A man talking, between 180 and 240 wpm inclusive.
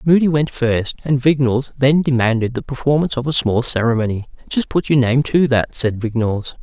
Yes: male; average, 190 wpm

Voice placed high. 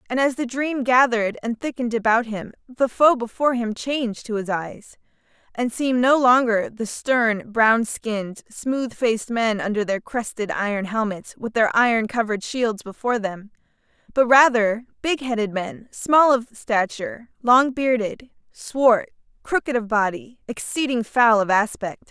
Yes: high, 230 Hz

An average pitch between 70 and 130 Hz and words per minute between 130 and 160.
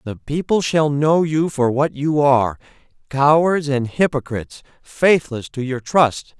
No: medium, 140 Hz; average, 140 wpm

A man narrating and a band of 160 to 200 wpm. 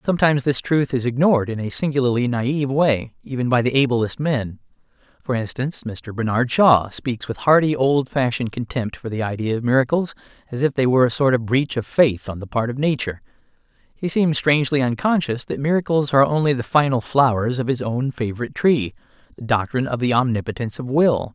Yes: male; average, 190 wpm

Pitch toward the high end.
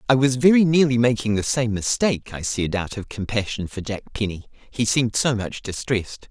No: low, 115 Hz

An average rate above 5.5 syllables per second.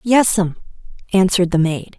Yes: 5.9 syllables/s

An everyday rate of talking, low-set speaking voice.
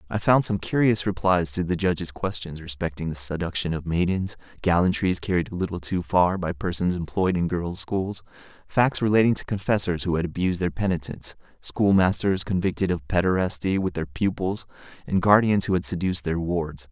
Yes: average, 175 wpm; very low, 90 Hz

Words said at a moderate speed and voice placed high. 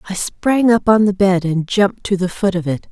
No: fast, 270 wpm; high, 195 Hz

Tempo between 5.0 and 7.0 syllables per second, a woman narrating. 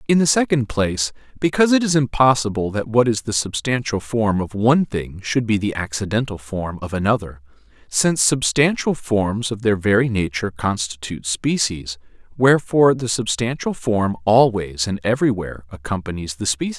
No: 5.4 syllables/s; male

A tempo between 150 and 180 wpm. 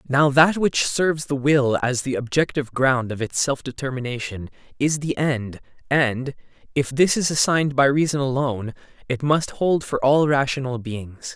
Yes: average, 170 wpm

